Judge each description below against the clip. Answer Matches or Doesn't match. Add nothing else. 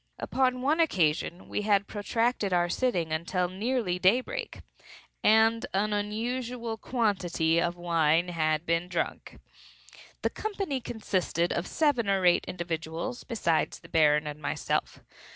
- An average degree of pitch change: Doesn't match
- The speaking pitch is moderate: Doesn't match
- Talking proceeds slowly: Matches